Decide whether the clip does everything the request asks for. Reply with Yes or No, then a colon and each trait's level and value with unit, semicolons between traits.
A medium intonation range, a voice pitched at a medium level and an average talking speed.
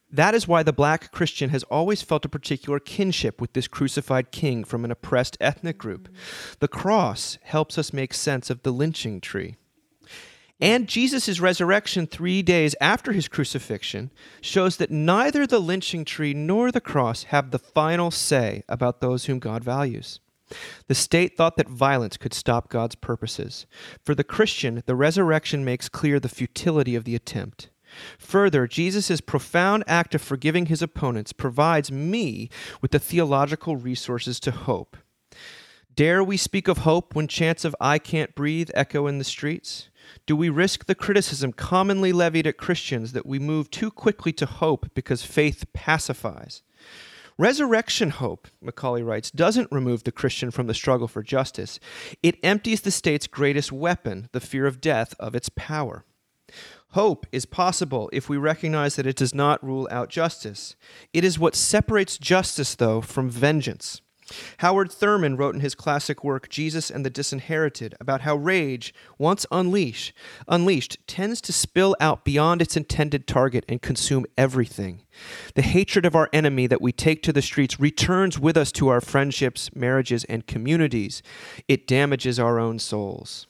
Yes: average, 5.0 semitones; medium, 145 Hz; average, 165 wpm